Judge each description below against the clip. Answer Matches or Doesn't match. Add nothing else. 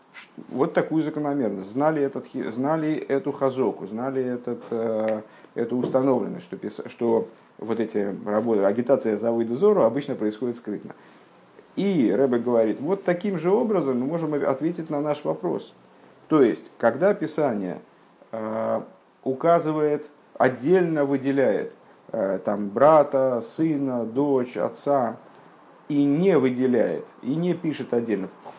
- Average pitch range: Matches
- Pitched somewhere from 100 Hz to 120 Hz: Doesn't match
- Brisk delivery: Doesn't match